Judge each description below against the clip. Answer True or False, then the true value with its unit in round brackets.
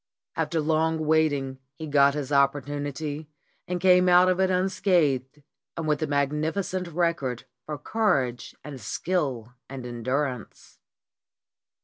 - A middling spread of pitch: True (3.9 semitones)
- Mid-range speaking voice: True (150 Hz)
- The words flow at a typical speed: False (120 wpm)